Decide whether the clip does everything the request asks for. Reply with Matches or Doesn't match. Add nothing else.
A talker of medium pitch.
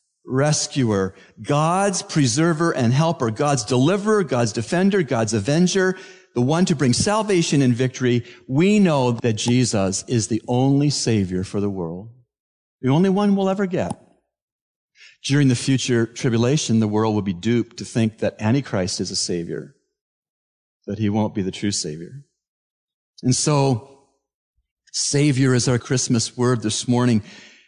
Doesn't match